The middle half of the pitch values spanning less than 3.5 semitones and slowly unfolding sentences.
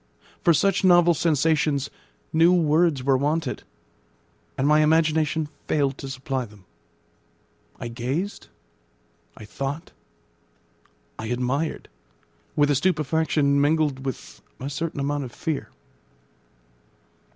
Yes: average, 3.1 semitones; slow, 105 wpm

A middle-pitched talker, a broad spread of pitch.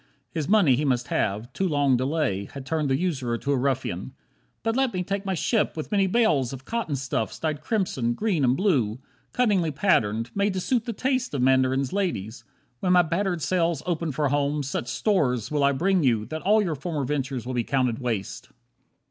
Yes: medium, 145 Hz; wide, 6.4 semitones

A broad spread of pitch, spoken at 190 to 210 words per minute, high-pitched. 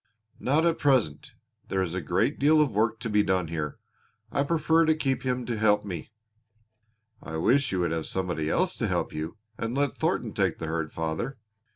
No: wide, 8.7 semitones; average, 200 wpm; low, 105 Hz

